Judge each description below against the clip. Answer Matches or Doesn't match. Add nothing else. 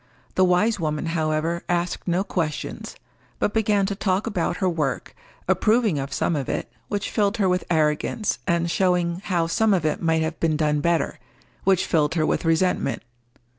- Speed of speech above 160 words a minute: Matches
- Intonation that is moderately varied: Matches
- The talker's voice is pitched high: Doesn't match